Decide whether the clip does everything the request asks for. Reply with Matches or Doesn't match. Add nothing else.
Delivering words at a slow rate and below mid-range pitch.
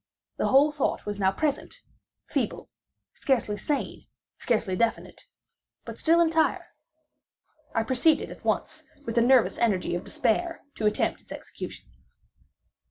Doesn't match